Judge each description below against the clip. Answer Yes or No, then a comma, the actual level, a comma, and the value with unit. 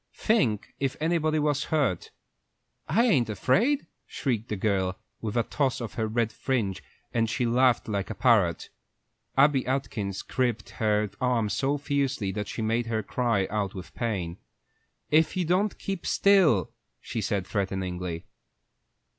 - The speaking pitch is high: No, low, 115 Hz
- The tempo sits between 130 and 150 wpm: Yes, average, 145 wpm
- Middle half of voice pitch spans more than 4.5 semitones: Yes, wide, 5.4 semitones